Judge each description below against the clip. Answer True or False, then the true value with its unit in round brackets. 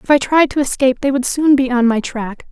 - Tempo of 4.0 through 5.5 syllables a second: False (6.0 syllables/s)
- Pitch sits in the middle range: False (265 Hz)